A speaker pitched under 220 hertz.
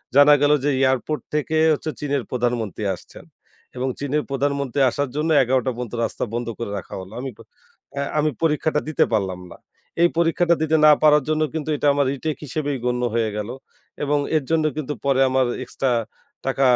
Yes: medium, 140 Hz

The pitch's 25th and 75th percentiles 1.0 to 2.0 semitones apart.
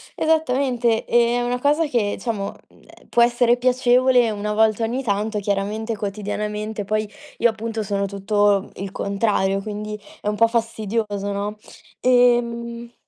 No: average, 2.7 semitones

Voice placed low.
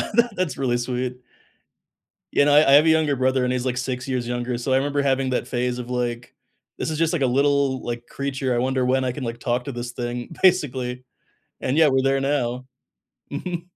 Yes: low, 130 Hz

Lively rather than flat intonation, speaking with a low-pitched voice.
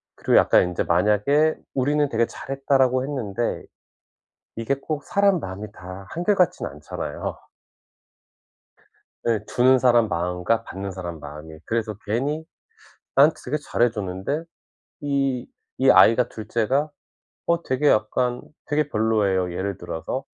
Yes: wide, 6.2 semitones; low, 120 Hz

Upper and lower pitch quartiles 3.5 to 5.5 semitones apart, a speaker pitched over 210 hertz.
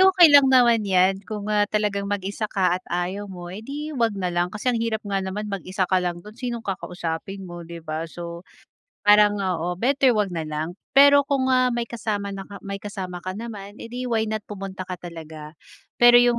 No: average, 4.2 semitones; high, 200 Hz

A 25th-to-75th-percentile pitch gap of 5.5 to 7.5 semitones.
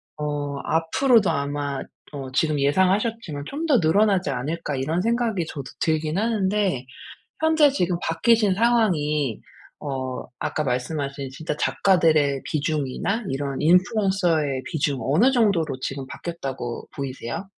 Yes: wide, 6.1 semitones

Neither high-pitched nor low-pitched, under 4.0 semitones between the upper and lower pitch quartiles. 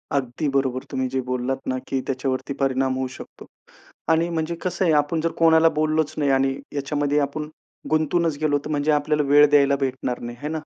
Yes: medium, 145 Hz; average, 2.7 semitones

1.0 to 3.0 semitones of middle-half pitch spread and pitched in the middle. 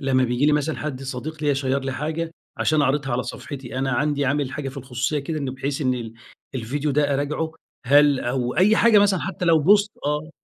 Yes: narrow, 2.6 semitones; medium, 145 Hz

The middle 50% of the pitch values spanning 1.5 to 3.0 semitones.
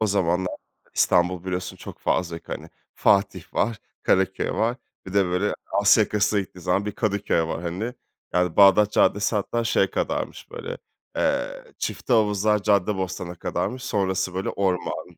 Yes: narrow, 2.6 semitones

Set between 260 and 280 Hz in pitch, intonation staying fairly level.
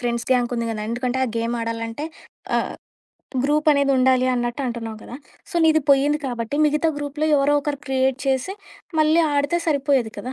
No: very high, 265 Hz; average, 3.3 semitones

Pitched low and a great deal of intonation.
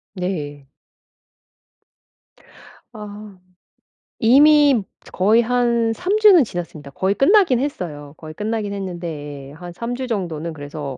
No: high, 200 Hz; wide, 7.5 semitones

